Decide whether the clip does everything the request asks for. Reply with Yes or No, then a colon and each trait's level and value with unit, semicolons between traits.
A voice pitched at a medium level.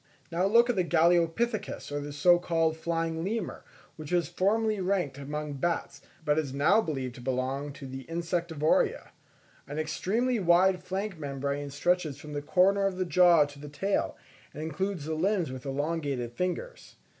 Yes: medium, 165 Hz